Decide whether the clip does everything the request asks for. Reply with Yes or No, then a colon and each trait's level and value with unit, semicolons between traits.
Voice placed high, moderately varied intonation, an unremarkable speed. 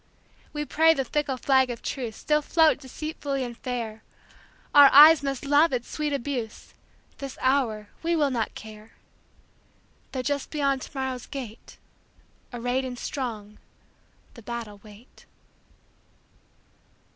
No: very high, 265 Hz; average, 3.4 semitones; slow, 110 wpm